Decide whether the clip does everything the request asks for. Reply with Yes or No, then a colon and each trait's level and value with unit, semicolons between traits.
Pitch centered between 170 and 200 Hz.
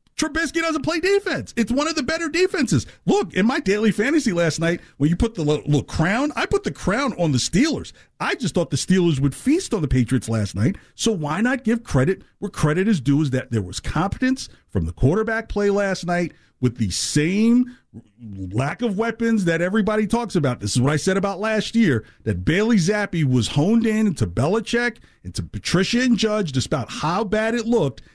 Yes: high, 190 Hz